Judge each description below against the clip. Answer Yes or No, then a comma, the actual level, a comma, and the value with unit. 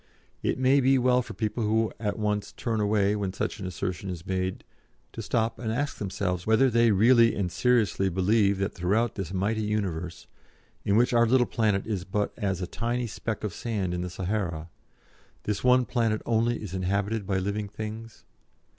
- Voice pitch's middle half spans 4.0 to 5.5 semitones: No, average, 3.2 semitones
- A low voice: Yes, low, 105 Hz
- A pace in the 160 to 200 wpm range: Yes, average, 185 wpm